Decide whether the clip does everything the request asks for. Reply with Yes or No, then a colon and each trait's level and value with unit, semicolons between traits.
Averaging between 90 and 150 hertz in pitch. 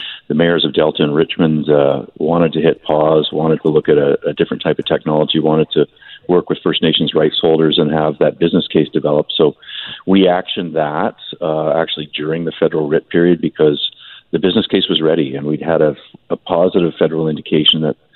No: very low, 80 Hz